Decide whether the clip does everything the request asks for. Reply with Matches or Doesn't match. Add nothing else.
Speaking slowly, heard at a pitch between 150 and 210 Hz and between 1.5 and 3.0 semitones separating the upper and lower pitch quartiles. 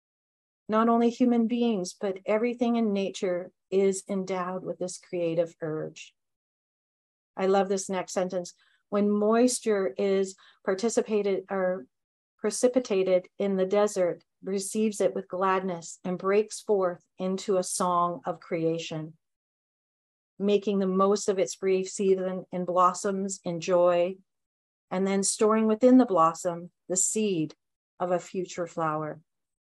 Matches